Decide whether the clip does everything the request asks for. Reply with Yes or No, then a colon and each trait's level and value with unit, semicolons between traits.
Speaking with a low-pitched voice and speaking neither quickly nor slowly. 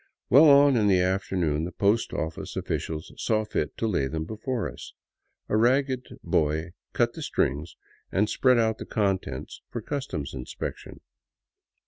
Yes: low, 100 Hz; average, 155 wpm